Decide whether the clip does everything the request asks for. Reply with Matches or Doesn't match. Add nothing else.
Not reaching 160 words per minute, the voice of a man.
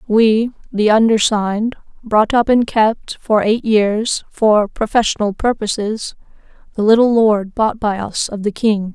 Doesn't match